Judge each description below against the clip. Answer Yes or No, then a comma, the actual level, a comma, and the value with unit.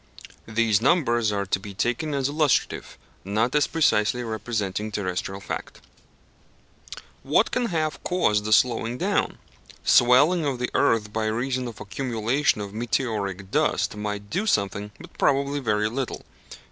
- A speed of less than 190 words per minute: Yes, average, 140 wpm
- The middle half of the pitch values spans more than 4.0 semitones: Yes, average, 4.5 semitones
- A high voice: No, low, 115 Hz